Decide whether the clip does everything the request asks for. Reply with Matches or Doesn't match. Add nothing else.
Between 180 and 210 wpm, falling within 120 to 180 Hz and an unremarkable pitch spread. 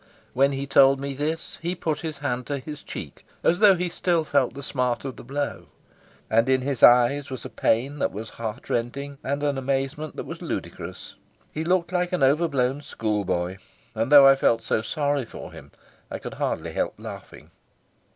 Matches